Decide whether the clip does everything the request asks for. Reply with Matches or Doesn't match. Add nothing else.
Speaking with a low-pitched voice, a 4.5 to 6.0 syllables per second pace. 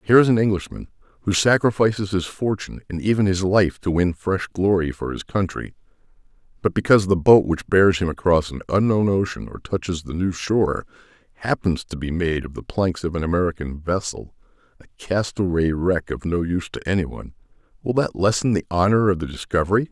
Matches